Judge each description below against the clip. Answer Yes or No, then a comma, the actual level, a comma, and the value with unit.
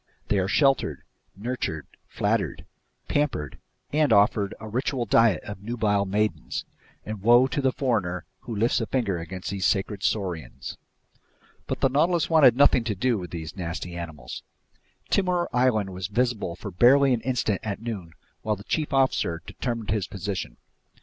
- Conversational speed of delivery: Yes, average, 155 wpm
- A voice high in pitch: No, low, 110 Hz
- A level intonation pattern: No, average, 5.0 semitones